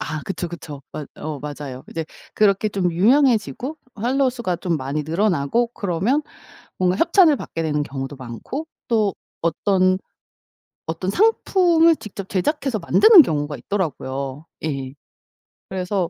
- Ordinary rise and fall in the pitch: No, wide, 8.0 semitones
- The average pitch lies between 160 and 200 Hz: Yes, medium, 185 Hz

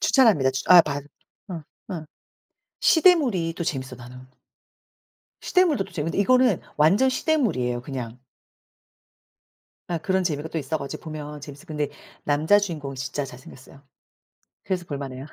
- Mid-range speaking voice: Yes, medium, 155 Hz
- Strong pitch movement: Yes, wide, 5.7 semitones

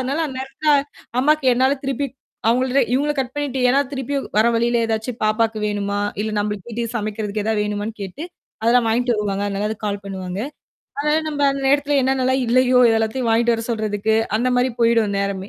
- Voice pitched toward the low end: No, high, 230 Hz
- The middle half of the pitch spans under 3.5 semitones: No, average, 3.8 semitones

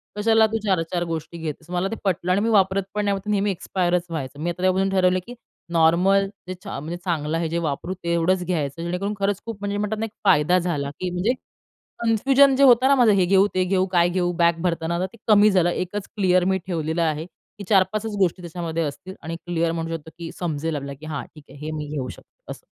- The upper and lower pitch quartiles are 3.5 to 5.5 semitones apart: No, average, 3.1 semitones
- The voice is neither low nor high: Yes, medium, 180 Hz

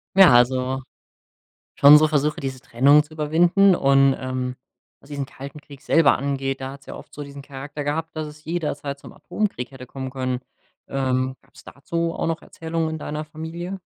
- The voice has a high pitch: No, medium, 140 Hz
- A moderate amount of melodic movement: Yes, average, 3.0 semitones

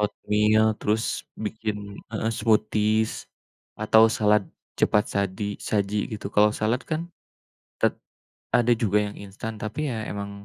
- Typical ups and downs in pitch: No, narrow, 1.1 semitones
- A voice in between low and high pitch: No, low, 105 Hz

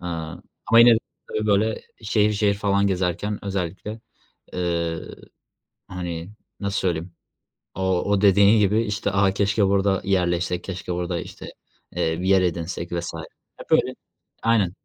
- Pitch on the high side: No, very low, 95 Hz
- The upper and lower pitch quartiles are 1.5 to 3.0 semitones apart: Yes, narrow, 2.6 semitones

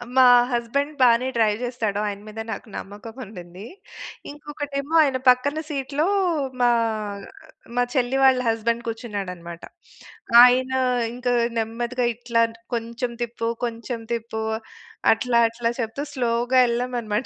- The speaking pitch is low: No, high, 235 Hz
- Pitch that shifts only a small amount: Yes, narrow, 2.2 semitones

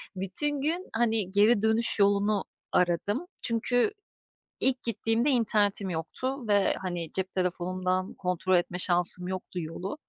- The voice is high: Yes, high, 200 Hz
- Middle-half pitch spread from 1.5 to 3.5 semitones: No, average, 4.1 semitones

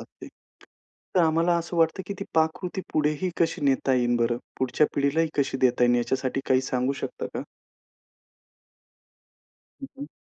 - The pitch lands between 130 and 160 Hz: Yes, medium, 140 Hz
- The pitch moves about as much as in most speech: Yes, average, 4.3 semitones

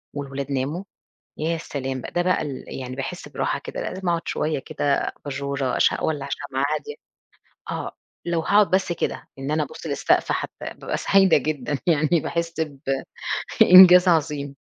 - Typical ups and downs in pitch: Yes, average, 3.8 semitones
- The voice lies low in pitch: No, medium, 155 Hz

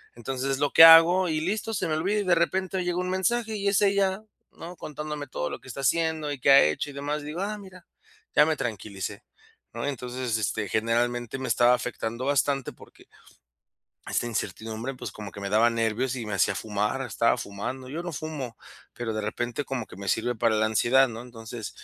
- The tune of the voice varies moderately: No, wide, 6.1 semitones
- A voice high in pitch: No, low, 130 Hz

